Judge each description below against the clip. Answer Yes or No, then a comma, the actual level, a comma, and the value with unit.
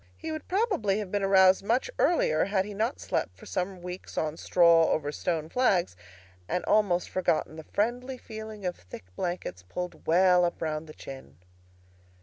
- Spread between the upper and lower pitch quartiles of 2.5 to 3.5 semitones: No, average, 4.6 semitones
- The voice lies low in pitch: No, medium, 185 Hz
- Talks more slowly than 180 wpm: Yes, average, 170 wpm